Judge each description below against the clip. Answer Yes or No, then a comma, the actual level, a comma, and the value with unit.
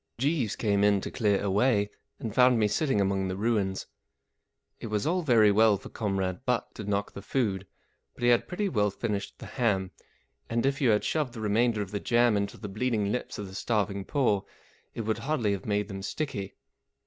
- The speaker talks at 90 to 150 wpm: No, fast, 205 wpm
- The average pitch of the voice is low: Yes, low, 105 Hz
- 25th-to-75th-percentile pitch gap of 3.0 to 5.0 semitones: Yes, average, 3.3 semitones